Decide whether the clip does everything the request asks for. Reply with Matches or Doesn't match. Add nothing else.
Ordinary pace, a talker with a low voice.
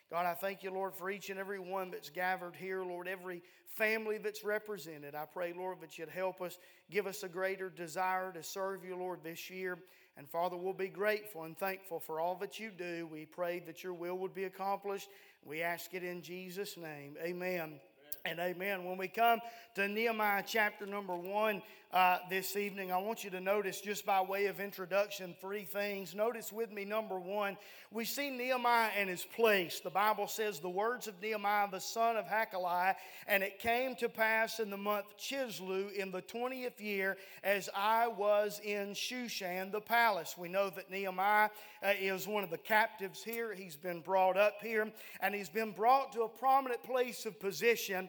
Doesn't match